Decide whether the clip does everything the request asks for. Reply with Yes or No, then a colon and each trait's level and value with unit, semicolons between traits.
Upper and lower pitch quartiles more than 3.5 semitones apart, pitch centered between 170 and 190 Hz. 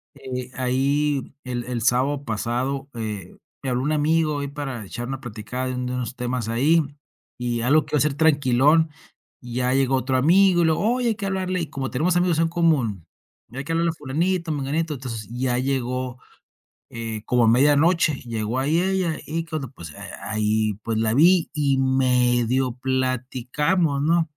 No: average, 4.2 semitones; low, 135 Hz